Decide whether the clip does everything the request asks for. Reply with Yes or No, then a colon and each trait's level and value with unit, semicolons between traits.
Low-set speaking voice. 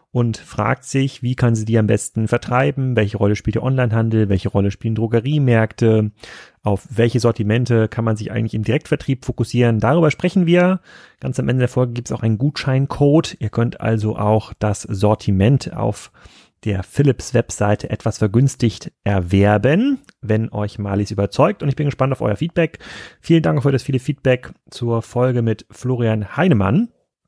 Yes: low, 115 Hz